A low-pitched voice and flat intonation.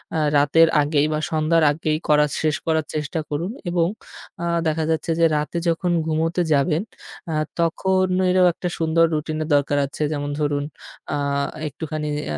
No: medium, 155 Hz; narrow, 1.9 semitones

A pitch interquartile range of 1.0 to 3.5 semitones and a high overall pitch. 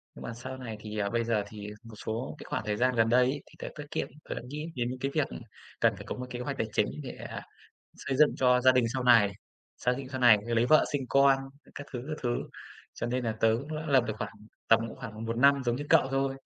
No: average, 2.9 semitones; low, 125 Hz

